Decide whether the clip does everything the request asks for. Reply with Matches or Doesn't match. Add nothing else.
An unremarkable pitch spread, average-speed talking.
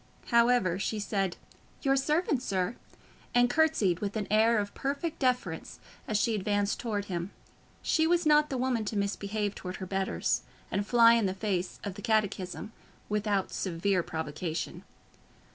Matches